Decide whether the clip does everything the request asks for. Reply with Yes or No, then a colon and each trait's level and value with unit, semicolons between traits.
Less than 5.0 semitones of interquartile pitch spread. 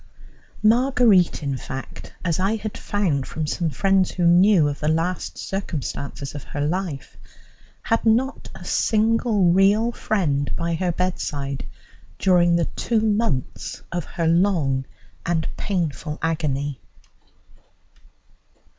No: average, 5.3 semitones